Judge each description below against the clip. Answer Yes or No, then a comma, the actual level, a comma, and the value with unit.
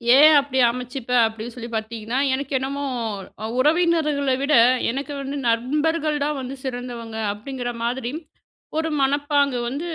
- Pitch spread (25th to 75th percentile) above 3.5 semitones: No, average, 3.2 semitones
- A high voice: Yes, very high, 265 Hz